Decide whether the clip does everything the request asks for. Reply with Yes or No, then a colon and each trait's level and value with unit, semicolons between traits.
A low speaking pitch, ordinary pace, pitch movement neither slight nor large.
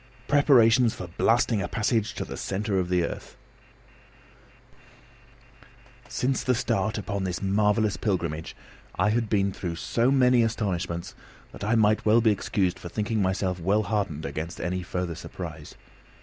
Yes: low, 100 Hz; average, 150 wpm; average, 3.8 semitones